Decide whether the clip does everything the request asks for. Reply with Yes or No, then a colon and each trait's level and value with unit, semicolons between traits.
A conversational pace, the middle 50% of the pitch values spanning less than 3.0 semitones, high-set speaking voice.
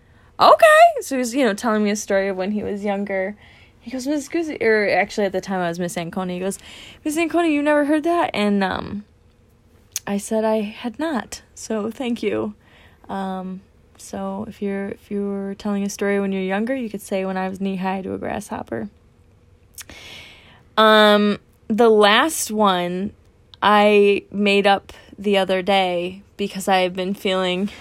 Yes: average, 180 wpm; narrow, 2.6 semitones; high, 200 Hz